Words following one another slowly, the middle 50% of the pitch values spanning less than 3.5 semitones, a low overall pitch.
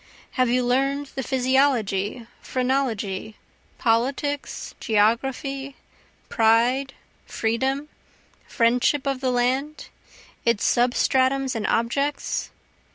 No: slow, 85 wpm; average, 2.8 semitones; very high, 255 Hz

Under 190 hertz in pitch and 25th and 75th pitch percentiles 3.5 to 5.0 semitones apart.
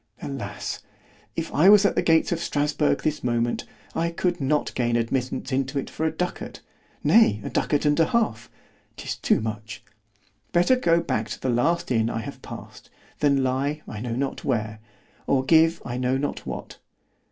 No: low, 135 Hz; wide, 5.5 semitones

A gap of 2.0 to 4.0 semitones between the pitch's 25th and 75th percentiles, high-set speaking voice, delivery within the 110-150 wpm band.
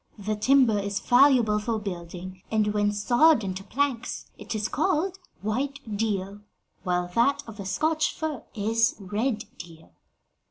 No: average, 4.8 semitones; high, 215 Hz; average, 145 wpm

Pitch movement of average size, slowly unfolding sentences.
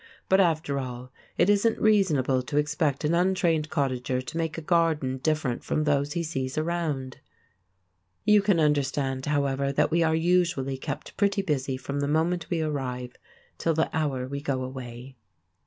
No: average, 3.9 semitones; average, 165 wpm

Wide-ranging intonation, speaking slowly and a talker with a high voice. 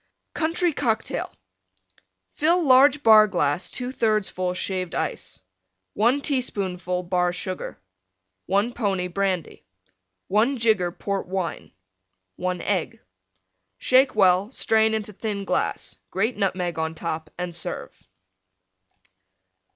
No: average, 4.3 semitones; slow, 105 wpm; high, 200 Hz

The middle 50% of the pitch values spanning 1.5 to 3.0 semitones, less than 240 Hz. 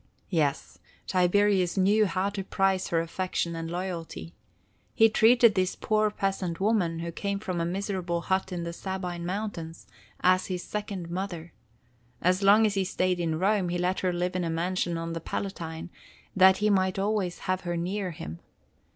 Yes: narrow, 2.5 semitones; medium, 185 Hz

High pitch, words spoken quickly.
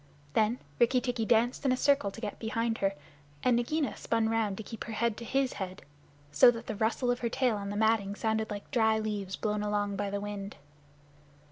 Yes: high, 220 Hz; fast, 215 wpm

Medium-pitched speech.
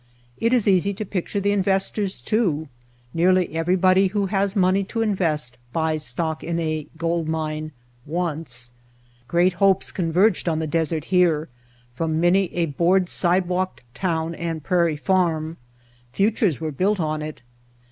Yes: medium, 170 Hz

